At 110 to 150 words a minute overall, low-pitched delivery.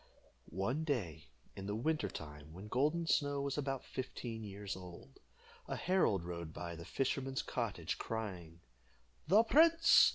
Yes: average, 140 wpm; low, 110 Hz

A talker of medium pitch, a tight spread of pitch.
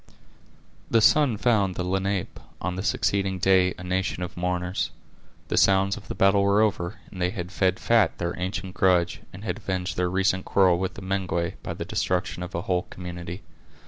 No: very low, 95 Hz; narrow, 1.5 semitones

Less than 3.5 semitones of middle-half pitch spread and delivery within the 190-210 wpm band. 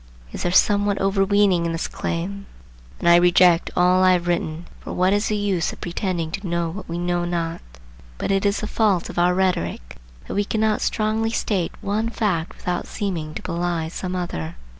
Yes: average, 2.8 semitones; average, 195 wpm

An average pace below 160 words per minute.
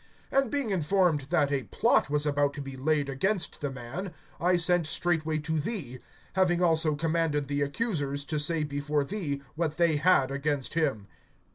No: average, 170 wpm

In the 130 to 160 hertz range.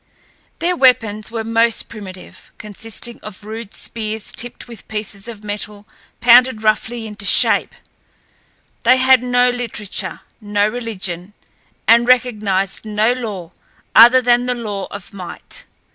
No: high, 220 Hz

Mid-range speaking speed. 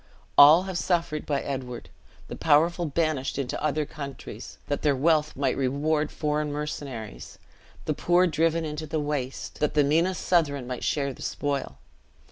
Yes: average, 155 wpm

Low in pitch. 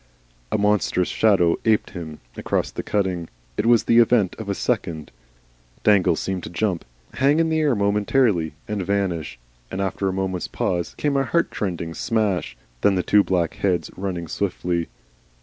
Yes: very low, 95 Hz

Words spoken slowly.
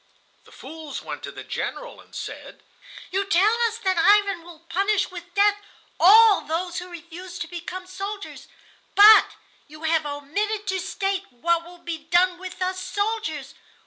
No: average, 160 wpm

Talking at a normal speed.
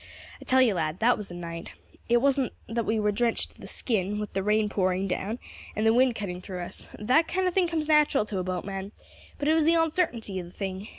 No: fast, 245 wpm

